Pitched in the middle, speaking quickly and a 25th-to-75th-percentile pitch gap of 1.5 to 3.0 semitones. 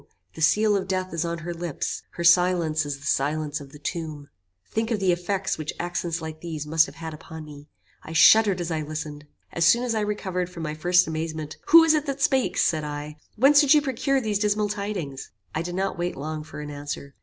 No: medium, 170 Hz; fast, 225 wpm; average, 4.7 semitones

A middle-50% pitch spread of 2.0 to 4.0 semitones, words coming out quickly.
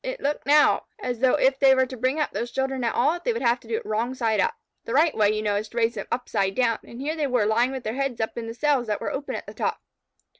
Yes: average, 3.3 semitones; fast, 300 wpm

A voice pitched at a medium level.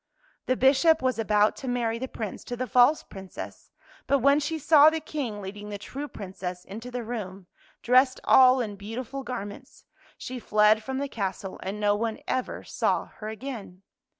No: high, 235 Hz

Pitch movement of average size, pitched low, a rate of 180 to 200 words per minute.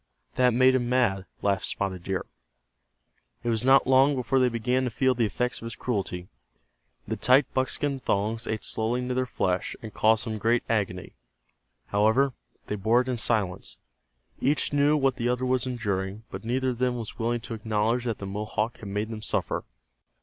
Yes: average, 3.2 semitones; low, 115 Hz; average, 185 wpm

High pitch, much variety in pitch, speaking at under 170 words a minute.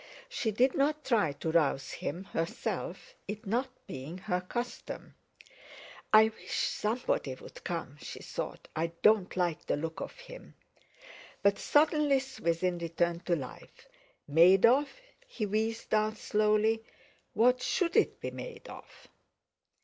Yes: high, 210 Hz; wide, 6.4 semitones; slow, 135 wpm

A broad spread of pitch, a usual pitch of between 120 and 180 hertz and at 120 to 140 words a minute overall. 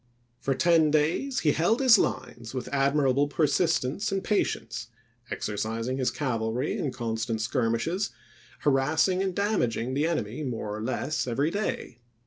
Yes: wide, 5.8 semitones; low, 135 Hz; slow, 135 wpm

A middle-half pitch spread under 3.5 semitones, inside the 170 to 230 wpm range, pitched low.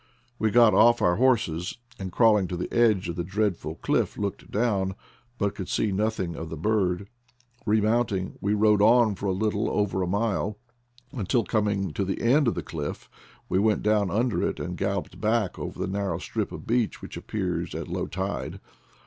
Yes: average, 2.8 semitones; average, 190 wpm; low, 100 Hz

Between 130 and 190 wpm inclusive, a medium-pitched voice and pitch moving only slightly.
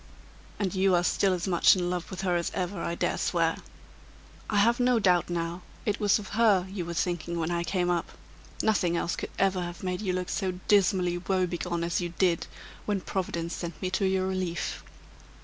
No: average, 200 wpm; medium, 180 Hz; narrow, 2.0 semitones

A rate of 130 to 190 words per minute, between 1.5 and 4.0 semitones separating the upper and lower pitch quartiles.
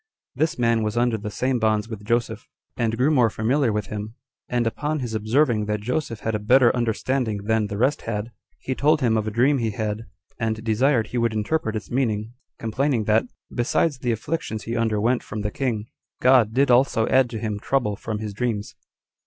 No: average, 200 wpm; average, 2.8 semitones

